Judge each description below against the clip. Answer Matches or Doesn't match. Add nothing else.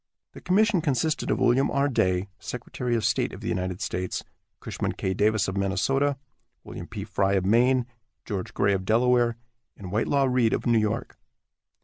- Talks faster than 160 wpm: Matches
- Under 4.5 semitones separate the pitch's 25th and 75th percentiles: Doesn't match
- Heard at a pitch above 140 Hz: Doesn't match